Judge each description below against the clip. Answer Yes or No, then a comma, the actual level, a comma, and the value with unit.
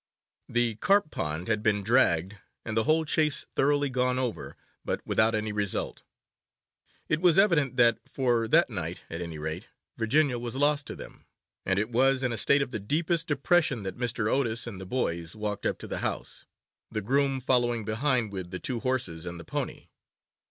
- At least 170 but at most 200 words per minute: Yes, average, 185 wpm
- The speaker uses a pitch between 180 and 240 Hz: No, low, 120 Hz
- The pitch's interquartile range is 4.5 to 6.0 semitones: Yes, average, 4.8 semitones